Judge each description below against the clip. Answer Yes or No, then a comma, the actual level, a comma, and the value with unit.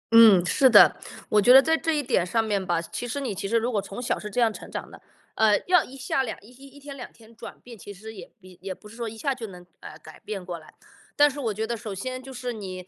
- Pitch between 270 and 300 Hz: No, high, 225 Hz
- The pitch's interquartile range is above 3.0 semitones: Yes, average, 4.5 semitones